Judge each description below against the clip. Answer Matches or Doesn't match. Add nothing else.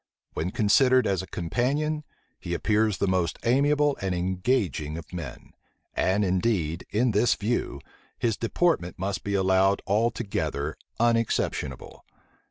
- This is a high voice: Doesn't match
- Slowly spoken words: Matches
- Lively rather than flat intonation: Doesn't match